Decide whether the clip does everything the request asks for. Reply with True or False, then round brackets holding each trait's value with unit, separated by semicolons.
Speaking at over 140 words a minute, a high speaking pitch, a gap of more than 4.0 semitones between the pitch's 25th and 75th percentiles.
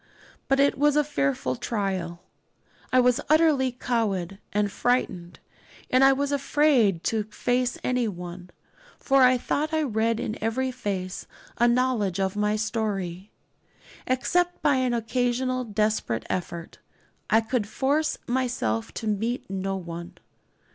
False (135 wpm; 230 Hz; 4.9 semitones)